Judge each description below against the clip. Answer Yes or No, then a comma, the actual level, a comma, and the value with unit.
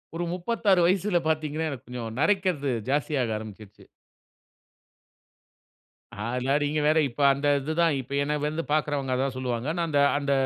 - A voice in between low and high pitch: Yes, medium, 145 Hz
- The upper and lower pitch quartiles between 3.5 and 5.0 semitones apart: Yes, average, 3.8 semitones